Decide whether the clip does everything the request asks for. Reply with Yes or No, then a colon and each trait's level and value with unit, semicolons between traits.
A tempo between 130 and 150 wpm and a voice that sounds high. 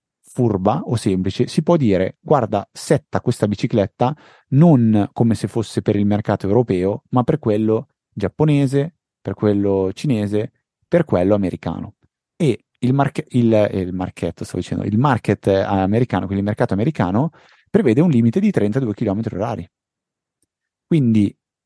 No: average, 145 wpm; low, 110 Hz